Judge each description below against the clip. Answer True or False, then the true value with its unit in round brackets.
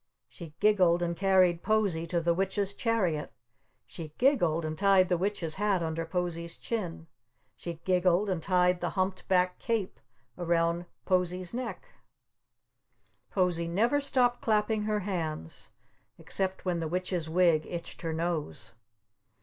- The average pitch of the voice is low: False (180 Hz)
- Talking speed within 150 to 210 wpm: False (135 wpm)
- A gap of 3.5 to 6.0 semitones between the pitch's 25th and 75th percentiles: False (2.9 semitones)